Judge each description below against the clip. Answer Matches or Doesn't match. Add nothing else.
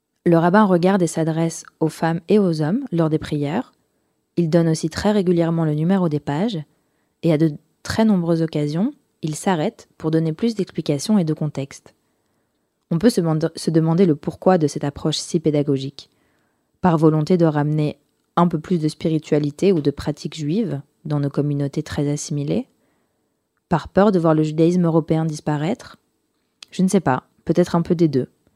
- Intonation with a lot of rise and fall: Doesn't match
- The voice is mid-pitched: Matches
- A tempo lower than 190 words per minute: Matches